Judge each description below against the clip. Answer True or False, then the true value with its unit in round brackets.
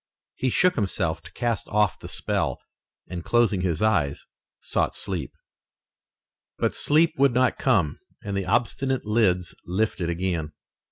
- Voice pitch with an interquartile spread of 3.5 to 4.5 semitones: False (5.3 semitones)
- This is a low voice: True (100 Hz)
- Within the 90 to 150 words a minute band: True (135 wpm)